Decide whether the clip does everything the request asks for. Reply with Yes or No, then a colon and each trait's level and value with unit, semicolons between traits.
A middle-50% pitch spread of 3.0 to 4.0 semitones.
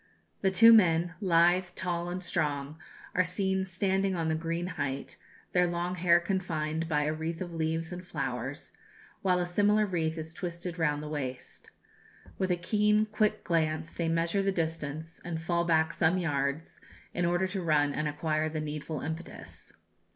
No: narrow, 2.6 semitones